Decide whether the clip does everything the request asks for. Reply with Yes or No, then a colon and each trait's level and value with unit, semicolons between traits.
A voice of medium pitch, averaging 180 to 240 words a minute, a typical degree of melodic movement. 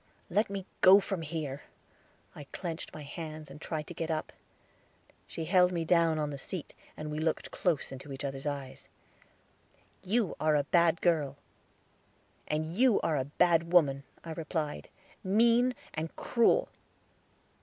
No: medium, 160 Hz; average, 155 wpm; average, 3.2 semitones